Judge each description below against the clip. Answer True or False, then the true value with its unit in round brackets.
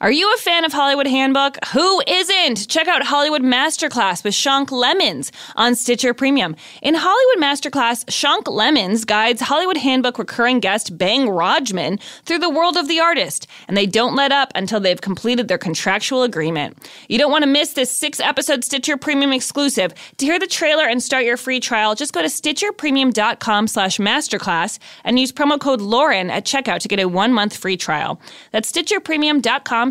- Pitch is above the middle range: True (265 Hz)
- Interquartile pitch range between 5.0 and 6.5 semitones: True (5.5 semitones)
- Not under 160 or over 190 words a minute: True (175 wpm)